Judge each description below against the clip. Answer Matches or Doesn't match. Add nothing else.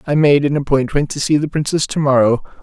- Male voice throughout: Matches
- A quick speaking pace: Matches